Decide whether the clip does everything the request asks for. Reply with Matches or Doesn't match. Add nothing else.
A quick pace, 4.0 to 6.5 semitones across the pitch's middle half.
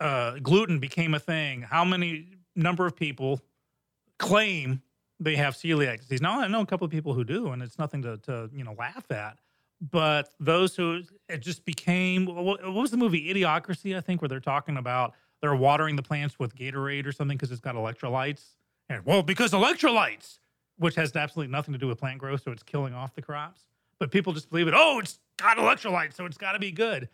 Matches